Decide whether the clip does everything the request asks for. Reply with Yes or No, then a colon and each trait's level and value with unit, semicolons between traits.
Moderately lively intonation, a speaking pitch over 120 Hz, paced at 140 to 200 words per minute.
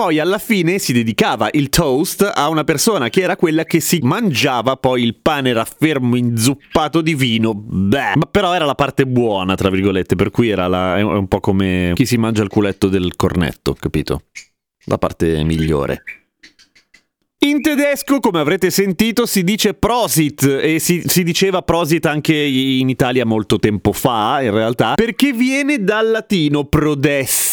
No: wide, 8.6 semitones; medium, 140 Hz; fast, 170 wpm